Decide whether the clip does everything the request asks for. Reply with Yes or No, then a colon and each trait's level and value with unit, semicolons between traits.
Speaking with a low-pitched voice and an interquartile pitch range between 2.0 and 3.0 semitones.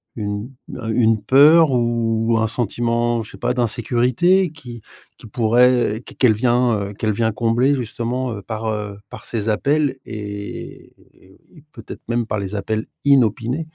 Yes: low, 115 Hz; narrow, 2.4 semitones